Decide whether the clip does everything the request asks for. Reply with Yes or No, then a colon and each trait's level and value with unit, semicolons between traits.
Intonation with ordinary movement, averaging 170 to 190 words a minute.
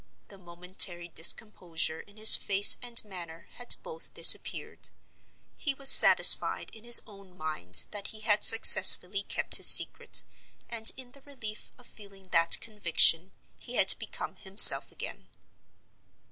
No: average, 4.5 semitones; average, 140 wpm